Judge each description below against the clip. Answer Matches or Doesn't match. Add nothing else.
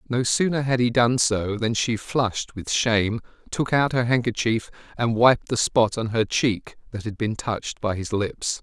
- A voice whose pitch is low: Matches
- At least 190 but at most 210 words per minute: Matches